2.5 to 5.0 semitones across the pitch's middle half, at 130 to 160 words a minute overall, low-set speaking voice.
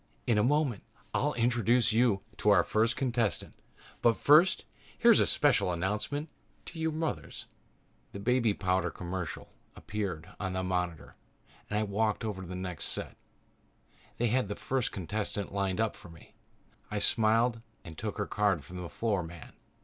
No: average, 4.1 semitones; average, 170 wpm; low, 105 Hz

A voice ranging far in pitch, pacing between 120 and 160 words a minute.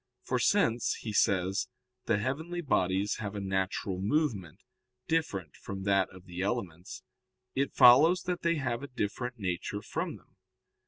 Yes: wide, 5.9 semitones; average, 150 wpm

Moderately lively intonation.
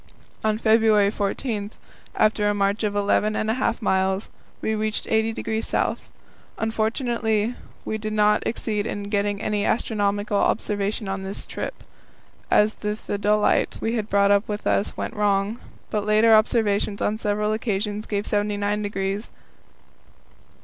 No: narrow, 1.3 semitones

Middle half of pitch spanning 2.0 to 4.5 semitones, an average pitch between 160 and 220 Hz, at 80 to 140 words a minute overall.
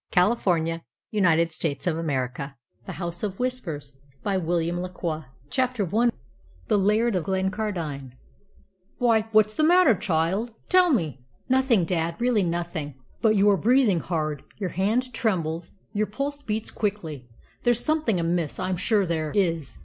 No: average, 5.2 semitones; medium, 185 Hz; slow, 135 wpm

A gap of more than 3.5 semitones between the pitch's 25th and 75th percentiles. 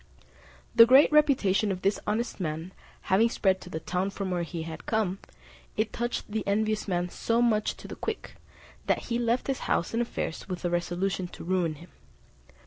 Yes: average, 4.3 semitones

